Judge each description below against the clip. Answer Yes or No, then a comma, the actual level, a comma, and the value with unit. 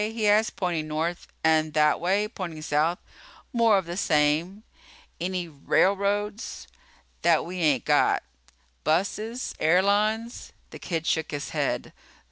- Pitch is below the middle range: No, medium, 180 Hz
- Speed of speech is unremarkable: No, slow, 125 wpm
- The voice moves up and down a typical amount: Yes, average, 4.7 semitones